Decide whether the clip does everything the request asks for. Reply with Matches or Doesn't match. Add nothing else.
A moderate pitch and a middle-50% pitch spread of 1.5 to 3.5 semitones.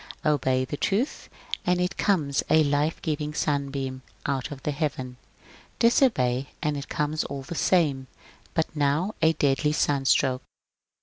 Matches